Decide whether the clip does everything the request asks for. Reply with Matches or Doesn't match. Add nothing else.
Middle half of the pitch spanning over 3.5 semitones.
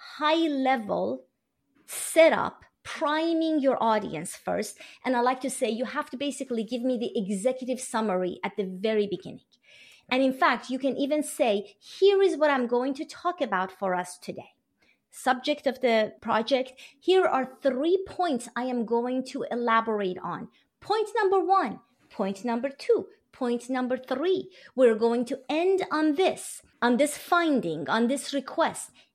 Matches